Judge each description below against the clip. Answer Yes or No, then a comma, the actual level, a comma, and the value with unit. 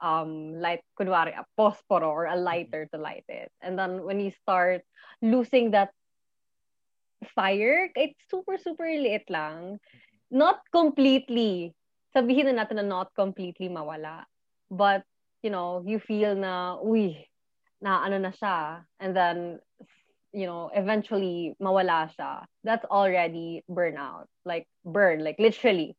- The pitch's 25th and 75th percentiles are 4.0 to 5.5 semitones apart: Yes, average, 4.4 semitones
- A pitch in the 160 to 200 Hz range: Yes, high, 190 Hz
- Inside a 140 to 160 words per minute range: No, average, 125 wpm